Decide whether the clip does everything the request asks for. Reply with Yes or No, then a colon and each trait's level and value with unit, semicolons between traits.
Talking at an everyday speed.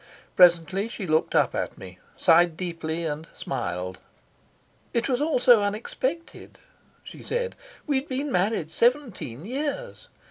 No: slow, 130 wpm